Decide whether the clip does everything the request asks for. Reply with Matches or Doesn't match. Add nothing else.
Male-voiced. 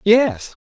Matches